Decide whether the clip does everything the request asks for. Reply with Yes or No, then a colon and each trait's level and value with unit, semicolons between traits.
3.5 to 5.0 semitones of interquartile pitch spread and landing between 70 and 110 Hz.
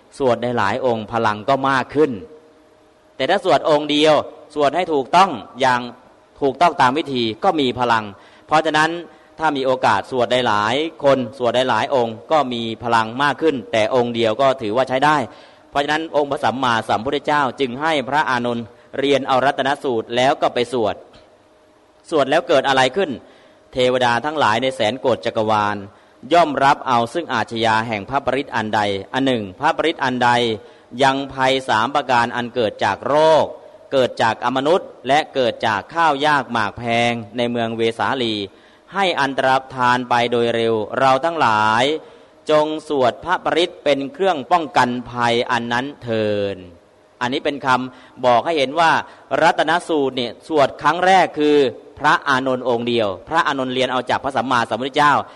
No: average, 4.2 semitones; low, 130 Hz